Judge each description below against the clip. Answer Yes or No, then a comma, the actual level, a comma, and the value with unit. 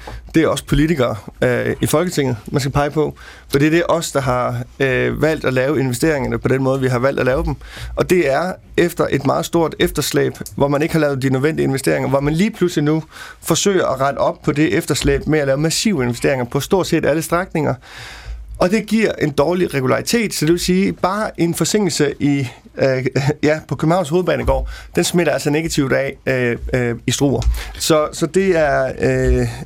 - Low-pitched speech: No, medium, 150 Hz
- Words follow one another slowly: No, average, 210 wpm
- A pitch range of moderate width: Yes, average, 3.8 semitones